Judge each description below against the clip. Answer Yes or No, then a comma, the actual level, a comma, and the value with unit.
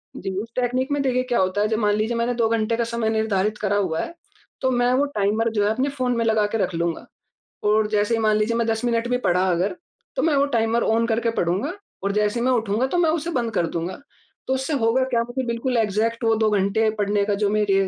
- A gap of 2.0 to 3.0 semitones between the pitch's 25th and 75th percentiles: Yes, average, 2.7 semitones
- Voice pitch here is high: Yes, high, 225 Hz